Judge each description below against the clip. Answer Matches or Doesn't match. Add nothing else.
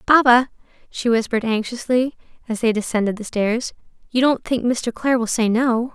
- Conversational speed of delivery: Matches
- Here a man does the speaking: Doesn't match